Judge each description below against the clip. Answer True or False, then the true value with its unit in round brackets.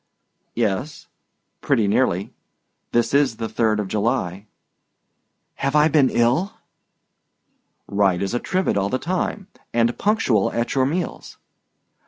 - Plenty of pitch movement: True (5.7 semitones)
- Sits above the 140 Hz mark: False (120 Hz)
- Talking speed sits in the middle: False (125 wpm)